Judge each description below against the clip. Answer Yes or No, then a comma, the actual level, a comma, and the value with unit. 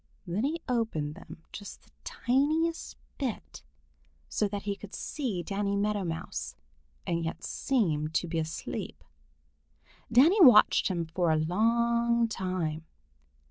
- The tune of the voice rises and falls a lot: Yes, wide, 6.1 semitones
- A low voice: No, high, 200 Hz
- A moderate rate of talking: No, slow, 130 wpm